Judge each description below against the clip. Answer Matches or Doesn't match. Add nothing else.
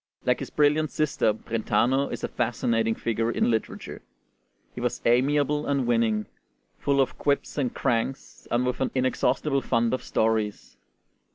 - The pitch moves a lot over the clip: Doesn't match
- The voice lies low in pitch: Matches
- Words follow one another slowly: Doesn't match